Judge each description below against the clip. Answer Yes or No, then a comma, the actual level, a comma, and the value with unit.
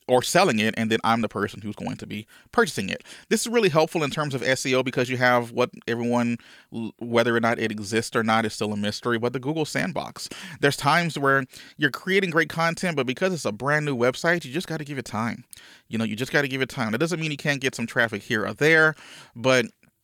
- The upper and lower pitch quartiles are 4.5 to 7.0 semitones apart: Yes, average, 5.3 semitones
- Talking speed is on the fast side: Yes, fast, 245 wpm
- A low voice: Yes, low, 130 Hz